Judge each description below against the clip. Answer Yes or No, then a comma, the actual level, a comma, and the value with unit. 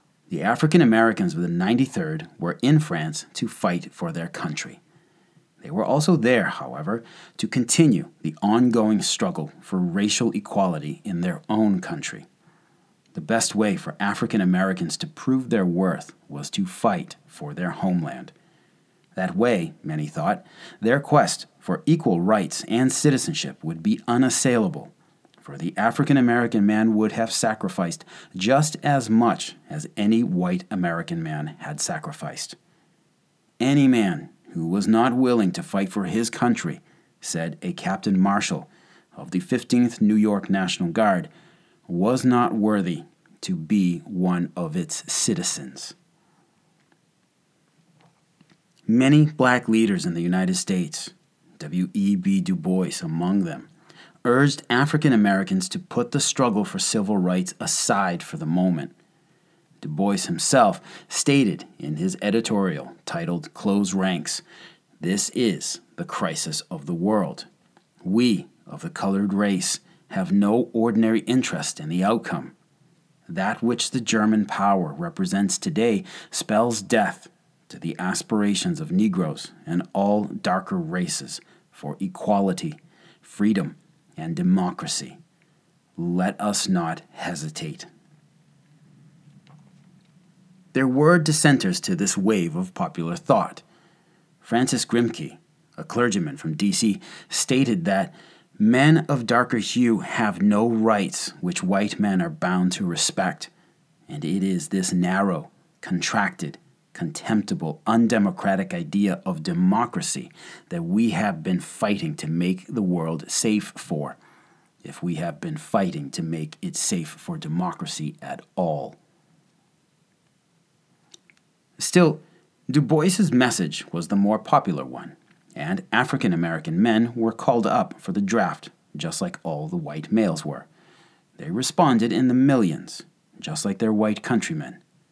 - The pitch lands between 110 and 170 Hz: Yes, medium, 140 Hz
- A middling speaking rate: No, slow, 130 wpm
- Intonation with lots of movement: Yes, wide, 8.7 semitones